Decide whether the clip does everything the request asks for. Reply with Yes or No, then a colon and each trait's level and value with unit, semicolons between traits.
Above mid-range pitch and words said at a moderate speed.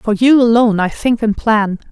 No: high, 225 Hz; fast, 220 wpm